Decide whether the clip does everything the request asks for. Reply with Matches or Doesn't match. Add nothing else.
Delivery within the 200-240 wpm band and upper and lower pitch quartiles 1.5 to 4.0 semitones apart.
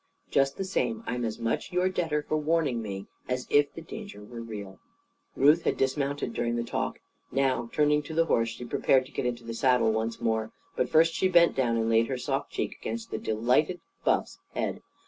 Doesn't match